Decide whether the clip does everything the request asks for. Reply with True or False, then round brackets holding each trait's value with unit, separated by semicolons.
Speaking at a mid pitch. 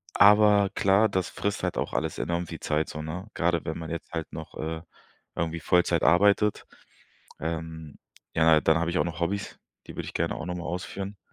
False (85 Hz)